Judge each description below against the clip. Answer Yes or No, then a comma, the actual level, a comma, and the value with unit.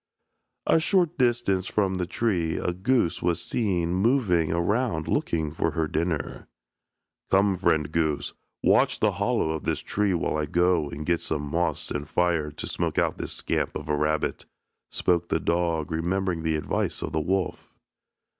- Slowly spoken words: No, average, 165 wpm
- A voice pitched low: Yes, very low, 85 Hz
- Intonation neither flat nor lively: Yes, average, 3.3 semitones